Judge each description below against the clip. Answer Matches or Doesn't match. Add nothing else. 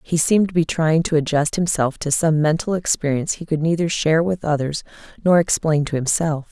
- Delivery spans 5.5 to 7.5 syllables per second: Matches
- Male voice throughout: Doesn't match